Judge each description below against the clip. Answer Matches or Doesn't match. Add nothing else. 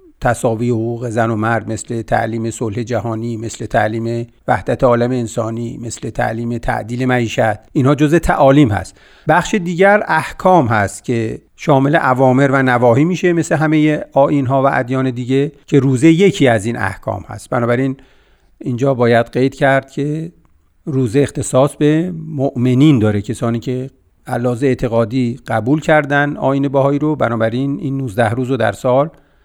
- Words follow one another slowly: Doesn't match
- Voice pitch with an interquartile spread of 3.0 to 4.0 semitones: Matches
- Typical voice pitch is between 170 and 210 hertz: Doesn't match